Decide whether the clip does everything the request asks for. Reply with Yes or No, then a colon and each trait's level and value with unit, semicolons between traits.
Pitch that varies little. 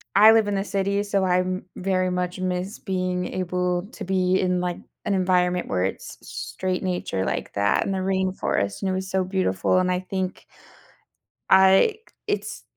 Yes: narrow, 1.1 semitones